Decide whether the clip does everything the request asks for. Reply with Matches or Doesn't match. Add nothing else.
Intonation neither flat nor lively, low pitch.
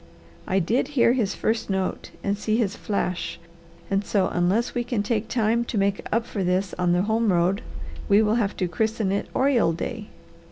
Doesn't match